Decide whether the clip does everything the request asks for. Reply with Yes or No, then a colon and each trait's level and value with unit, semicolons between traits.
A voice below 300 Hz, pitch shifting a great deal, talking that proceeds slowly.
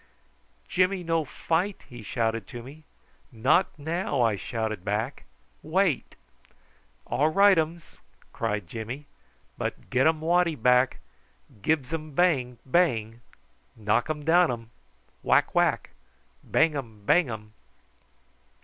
Yes: medium, 140 Hz; wide, 6.3 semitones; slow, 100 wpm